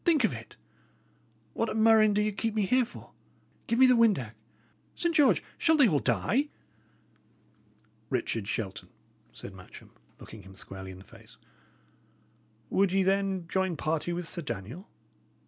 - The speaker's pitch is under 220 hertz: Yes, high, 190 Hz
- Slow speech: No, average, 155 wpm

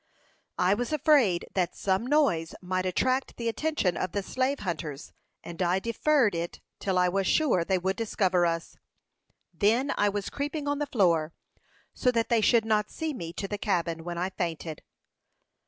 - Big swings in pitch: Yes, wide, 5.9 semitones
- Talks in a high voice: Yes, high, 195 Hz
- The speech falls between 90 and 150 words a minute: No, average, 175 wpm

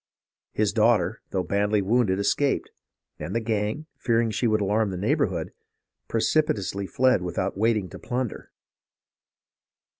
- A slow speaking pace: Yes, slow, 130 wpm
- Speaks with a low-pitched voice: Yes, low, 110 Hz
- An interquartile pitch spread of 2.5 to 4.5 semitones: Yes, average, 3.2 semitones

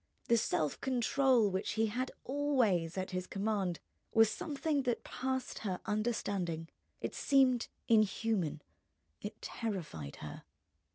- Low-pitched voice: No, high, 215 Hz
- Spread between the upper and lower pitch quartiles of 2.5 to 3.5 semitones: No, wide, 5.6 semitones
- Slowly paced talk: Yes, slow, 120 wpm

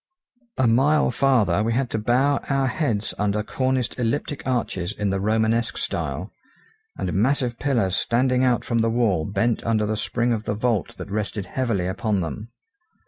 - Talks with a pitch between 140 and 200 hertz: No, low, 115 Hz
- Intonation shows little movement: No, average, 3.4 semitones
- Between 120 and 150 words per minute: No, average, 170 wpm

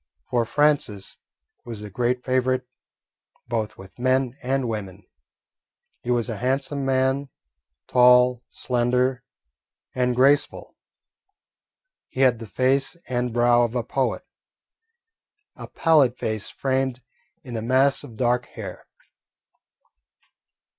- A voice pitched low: Yes, low, 125 Hz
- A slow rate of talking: Yes, slow, 115 wpm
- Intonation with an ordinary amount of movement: No, narrow, 1.8 semitones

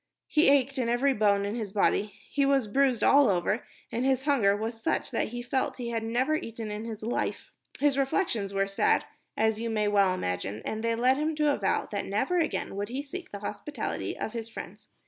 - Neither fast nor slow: No, fast, 220 wpm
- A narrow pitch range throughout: No, average, 4.6 semitones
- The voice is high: Yes, high, 230 Hz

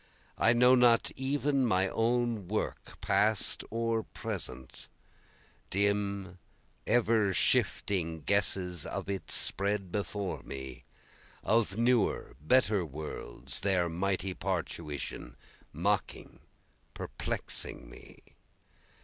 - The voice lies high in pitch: No, low, 100 Hz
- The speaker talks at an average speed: No, slow, 90 wpm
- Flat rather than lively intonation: No, average, 4.3 semitones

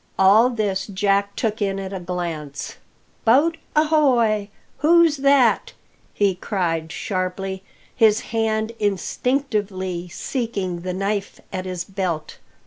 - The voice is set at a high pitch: Yes, high, 200 Hz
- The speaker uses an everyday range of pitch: Yes, average, 3.9 semitones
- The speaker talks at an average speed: No, slow, 115 wpm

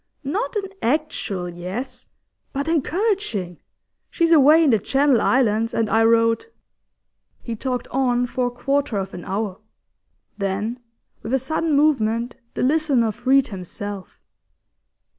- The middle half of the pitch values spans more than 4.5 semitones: Yes, average, 5.0 semitones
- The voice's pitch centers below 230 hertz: No, high, 245 Hz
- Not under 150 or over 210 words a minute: No, slow, 135 wpm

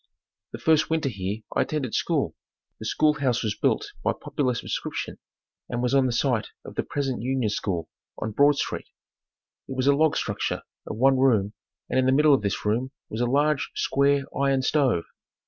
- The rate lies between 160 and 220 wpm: Yes, average, 190 wpm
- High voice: No, low, 130 Hz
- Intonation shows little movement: No, average, 3.8 semitones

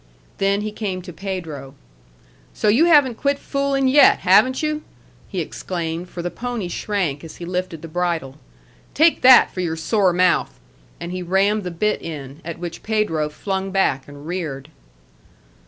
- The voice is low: No, medium, 185 Hz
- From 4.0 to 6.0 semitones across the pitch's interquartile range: Yes, average, 4.5 semitones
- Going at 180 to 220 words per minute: No, average, 165 wpm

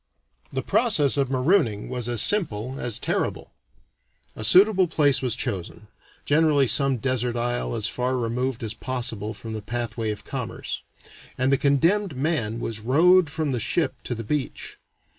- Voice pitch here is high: No, low, 130 Hz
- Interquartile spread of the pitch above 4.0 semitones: Yes, average, 4.4 semitones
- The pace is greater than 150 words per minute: Yes, average, 160 wpm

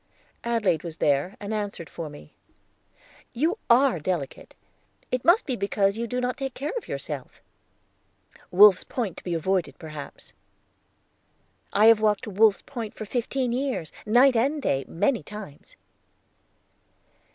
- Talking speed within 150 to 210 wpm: No, average, 140 wpm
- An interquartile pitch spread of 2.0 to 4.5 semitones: No, wide, 5.6 semitones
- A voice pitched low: No, high, 215 Hz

